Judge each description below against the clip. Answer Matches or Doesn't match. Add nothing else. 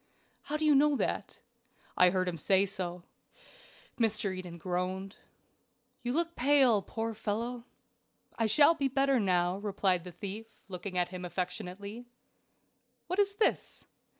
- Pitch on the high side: Matches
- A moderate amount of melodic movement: Doesn't match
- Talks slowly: Doesn't match